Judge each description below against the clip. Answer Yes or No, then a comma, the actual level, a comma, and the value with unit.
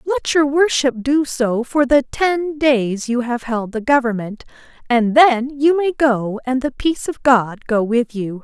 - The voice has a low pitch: No, very high, 260 Hz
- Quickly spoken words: No, average, 190 wpm